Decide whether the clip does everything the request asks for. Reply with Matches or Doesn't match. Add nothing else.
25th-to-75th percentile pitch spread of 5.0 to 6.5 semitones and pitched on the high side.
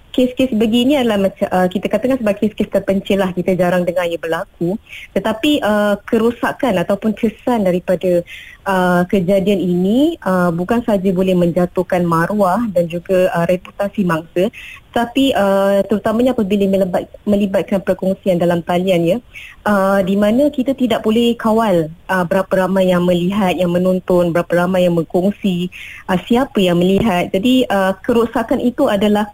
Doesn't match